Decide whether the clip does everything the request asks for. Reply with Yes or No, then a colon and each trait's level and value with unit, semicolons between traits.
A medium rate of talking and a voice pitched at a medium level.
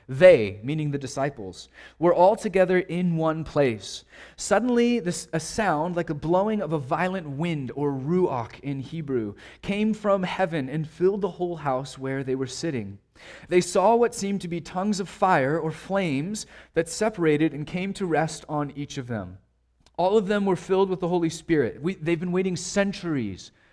Yes: average, 180 wpm; medium, 165 Hz